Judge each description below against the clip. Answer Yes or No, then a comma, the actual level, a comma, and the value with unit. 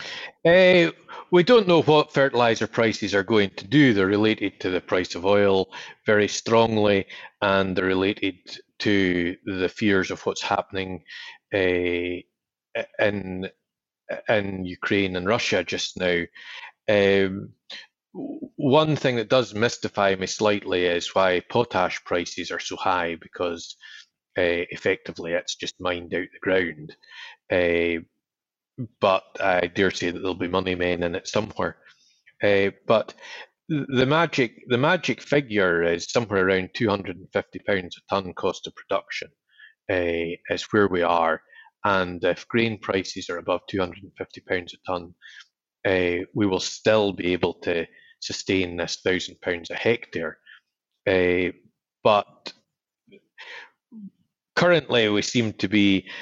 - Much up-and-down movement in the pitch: No, average, 4.8 semitones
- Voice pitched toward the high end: No, low, 100 Hz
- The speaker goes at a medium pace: No, slow, 130 wpm